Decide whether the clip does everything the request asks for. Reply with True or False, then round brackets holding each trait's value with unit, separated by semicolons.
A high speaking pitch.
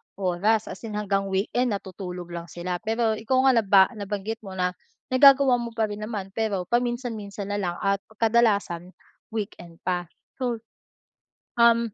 True (205 Hz)